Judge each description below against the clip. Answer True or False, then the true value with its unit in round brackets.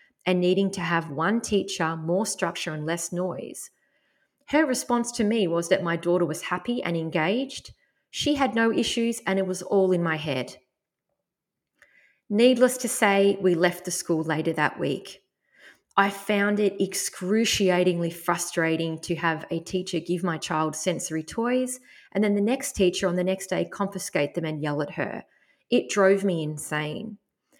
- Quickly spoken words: False (165 wpm)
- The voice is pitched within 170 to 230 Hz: True (190 Hz)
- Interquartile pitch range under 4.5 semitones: False (4.9 semitones)